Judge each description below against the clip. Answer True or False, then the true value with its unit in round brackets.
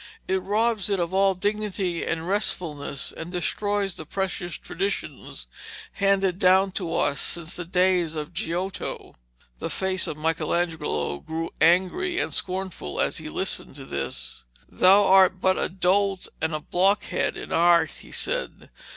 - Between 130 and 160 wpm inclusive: True (150 wpm)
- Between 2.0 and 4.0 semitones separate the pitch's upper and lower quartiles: True (2.8 semitones)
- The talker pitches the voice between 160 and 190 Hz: True (185 Hz)